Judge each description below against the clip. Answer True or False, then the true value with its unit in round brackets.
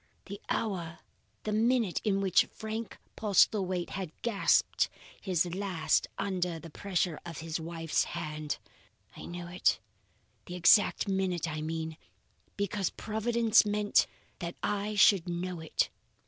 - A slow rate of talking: True (130 wpm)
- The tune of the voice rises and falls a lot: False (3.5 semitones)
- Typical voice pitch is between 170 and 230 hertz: True (185 Hz)